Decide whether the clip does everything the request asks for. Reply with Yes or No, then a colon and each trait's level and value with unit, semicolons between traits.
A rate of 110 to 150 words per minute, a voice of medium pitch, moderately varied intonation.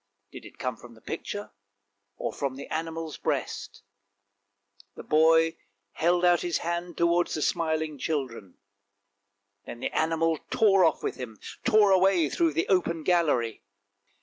Yes: average, 145 wpm; medium, 165 Hz; average, 3.3 semitones